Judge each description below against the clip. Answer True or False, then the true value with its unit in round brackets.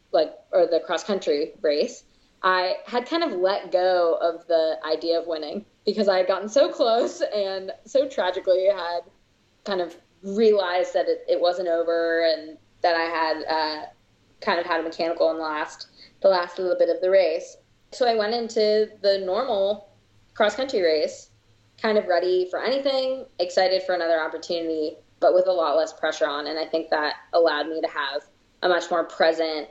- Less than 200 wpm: True (185 wpm)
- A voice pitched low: False (180 Hz)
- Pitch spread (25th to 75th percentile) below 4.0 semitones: False (4.3 semitones)